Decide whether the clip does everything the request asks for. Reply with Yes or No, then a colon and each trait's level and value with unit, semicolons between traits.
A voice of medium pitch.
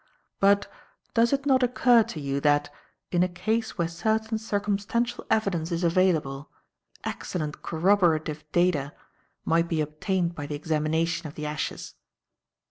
Yes: medium, 175 Hz